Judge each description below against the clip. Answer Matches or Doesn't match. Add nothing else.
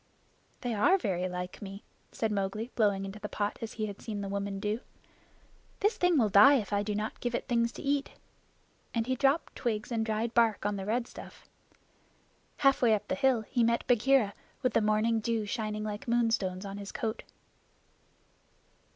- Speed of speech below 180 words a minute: Doesn't match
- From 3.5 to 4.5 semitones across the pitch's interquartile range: Doesn't match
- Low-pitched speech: Doesn't match